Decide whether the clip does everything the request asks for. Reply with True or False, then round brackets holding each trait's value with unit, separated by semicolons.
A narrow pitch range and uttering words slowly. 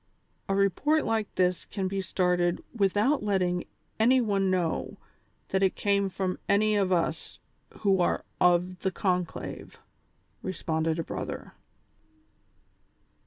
True (2.2 semitones; 125 wpm)